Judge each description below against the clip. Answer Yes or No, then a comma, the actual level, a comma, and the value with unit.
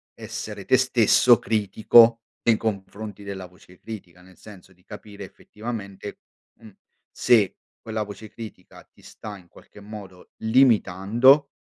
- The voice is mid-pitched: No, low, 105 Hz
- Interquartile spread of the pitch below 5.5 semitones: Yes, average, 2.8 semitones